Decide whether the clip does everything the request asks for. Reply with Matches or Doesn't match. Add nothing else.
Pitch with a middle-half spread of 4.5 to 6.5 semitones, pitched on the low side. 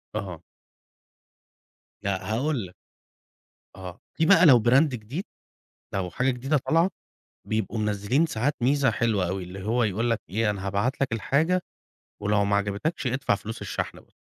Matches